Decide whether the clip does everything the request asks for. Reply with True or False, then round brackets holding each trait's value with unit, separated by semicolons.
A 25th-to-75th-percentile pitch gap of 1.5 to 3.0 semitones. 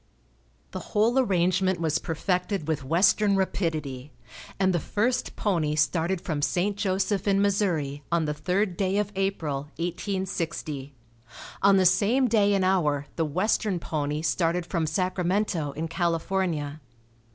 False (3.8 semitones)